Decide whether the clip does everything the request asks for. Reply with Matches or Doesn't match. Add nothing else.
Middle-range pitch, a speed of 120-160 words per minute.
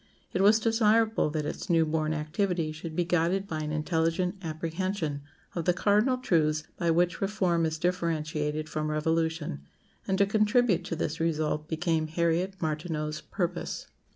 Matches